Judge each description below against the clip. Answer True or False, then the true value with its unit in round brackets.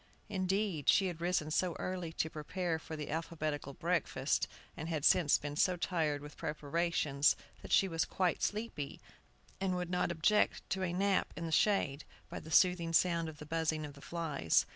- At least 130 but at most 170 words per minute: False (185 wpm)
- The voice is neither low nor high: True (165 Hz)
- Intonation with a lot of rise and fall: False (3.1 semitones)